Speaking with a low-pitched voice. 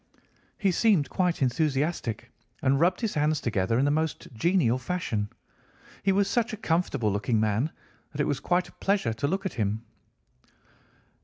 No: medium, 150 Hz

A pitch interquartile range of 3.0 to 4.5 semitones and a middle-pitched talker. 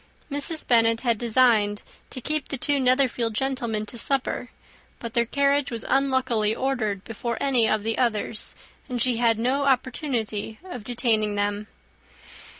No: average, 3.3 semitones; high, 240 Hz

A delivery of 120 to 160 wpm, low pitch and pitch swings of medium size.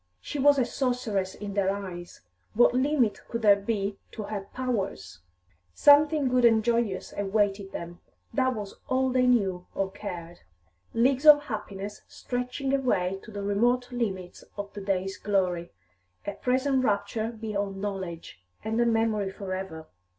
No: average, 150 wpm; high, 210 Hz; average, 4.3 semitones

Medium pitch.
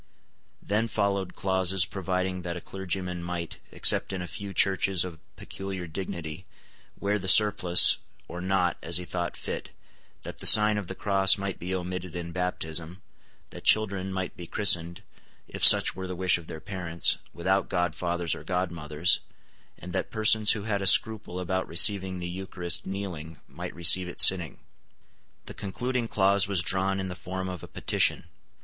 No: very low, 95 Hz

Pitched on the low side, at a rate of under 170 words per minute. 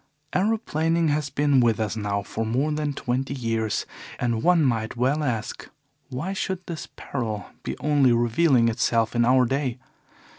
Yes: low, 130 Hz; average, 155 wpm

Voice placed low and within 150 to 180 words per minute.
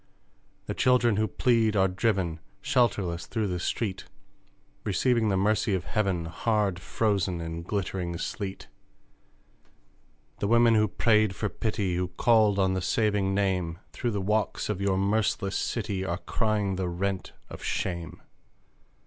No: low, 100 Hz; average, 140 wpm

